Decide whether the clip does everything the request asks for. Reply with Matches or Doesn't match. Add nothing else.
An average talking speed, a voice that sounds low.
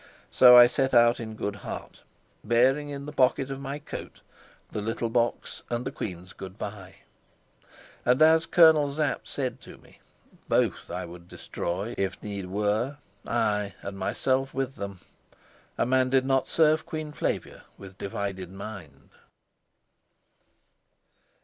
Matches